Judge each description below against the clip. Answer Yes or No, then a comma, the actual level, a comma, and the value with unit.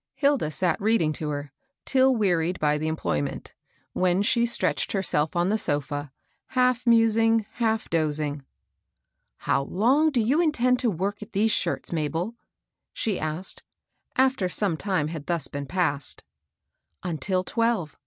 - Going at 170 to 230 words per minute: No, average, 155 wpm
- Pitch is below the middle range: No, medium, 185 Hz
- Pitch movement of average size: No, wide, 6.8 semitones